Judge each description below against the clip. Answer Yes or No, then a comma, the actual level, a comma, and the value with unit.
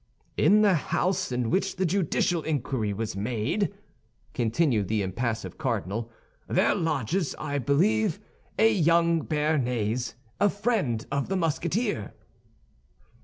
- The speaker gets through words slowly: Yes, slow, 120 wpm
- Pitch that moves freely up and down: Yes, wide, 7.8 semitones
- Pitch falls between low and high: Yes, medium, 145 Hz